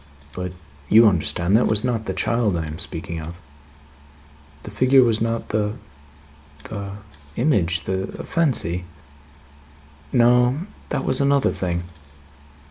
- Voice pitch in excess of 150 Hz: No, low, 105 Hz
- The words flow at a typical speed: No, slow, 130 wpm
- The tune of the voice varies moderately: No, wide, 5.7 semitones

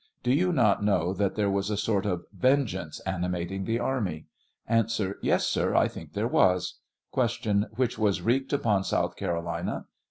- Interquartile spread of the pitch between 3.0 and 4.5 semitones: Yes, average, 4.1 semitones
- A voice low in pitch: Yes, low, 100 Hz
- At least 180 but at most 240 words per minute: No, average, 170 wpm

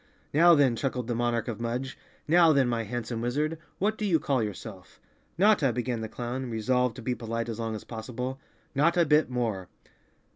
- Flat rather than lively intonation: No, average, 3.8 semitones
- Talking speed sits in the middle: Yes, average, 185 wpm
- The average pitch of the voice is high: No, low, 125 Hz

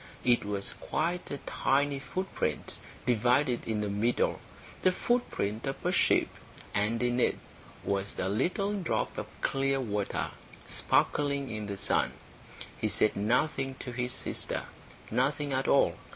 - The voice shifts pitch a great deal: No, average, 4.8 semitones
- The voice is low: Yes, low, 125 Hz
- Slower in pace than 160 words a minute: Yes, average, 140 wpm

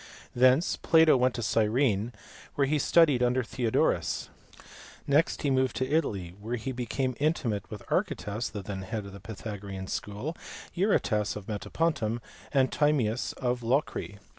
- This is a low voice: Yes, low, 120 Hz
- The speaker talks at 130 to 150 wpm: Yes, average, 145 wpm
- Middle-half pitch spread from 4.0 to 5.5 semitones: Yes, average, 4.7 semitones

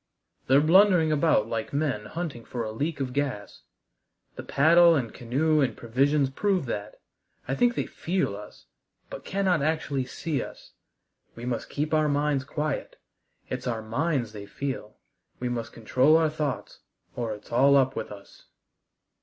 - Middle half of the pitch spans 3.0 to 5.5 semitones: Yes, average, 4.8 semitones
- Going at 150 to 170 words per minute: Yes, average, 160 wpm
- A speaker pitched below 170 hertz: Yes, medium, 140 Hz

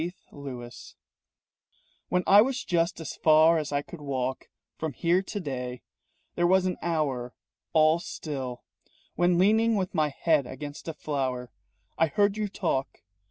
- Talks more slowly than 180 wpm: Yes, average, 155 wpm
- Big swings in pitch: No, average, 4.7 semitones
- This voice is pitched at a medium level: Yes, medium, 160 Hz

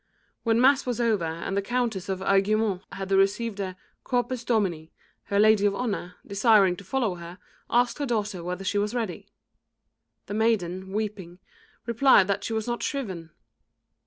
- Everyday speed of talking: Yes, average, 160 wpm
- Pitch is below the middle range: No, high, 205 Hz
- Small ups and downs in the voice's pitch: No, average, 3.5 semitones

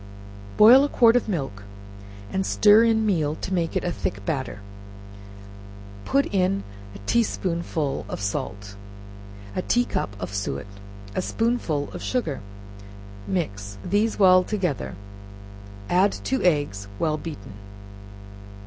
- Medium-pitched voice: Yes, medium, 175 Hz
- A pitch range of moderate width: No, wide, 8.0 semitones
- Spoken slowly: Yes, slow, 130 wpm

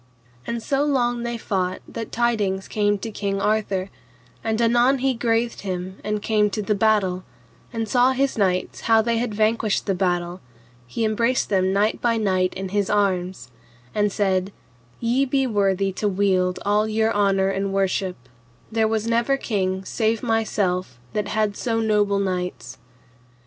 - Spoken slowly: No, average, 160 wpm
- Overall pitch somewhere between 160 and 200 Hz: No, high, 210 Hz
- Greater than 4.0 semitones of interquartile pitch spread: No, average, 3.0 semitones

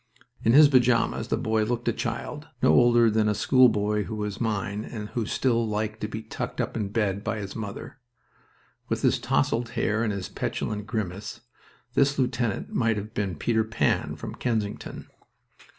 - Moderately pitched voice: No, low, 110 Hz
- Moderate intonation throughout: No, narrow, 2.2 semitones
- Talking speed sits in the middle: Yes, average, 175 wpm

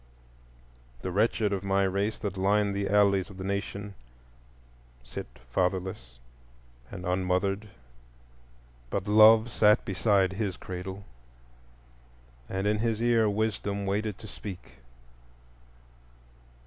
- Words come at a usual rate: No, slow, 110 wpm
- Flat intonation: Yes, narrow, 1.9 semitones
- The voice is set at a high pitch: No, low, 100 Hz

